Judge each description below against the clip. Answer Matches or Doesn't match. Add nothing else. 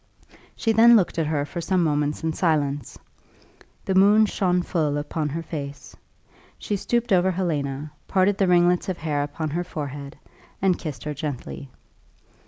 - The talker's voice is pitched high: Doesn't match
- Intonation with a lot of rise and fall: Doesn't match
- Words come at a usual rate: Matches